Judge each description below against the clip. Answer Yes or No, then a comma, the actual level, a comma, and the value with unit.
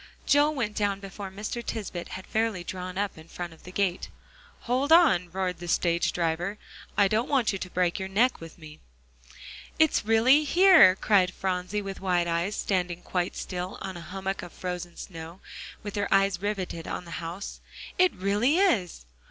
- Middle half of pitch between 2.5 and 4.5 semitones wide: Yes, average, 3.2 semitones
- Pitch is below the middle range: No, high, 190 Hz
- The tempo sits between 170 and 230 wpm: Yes, average, 180 wpm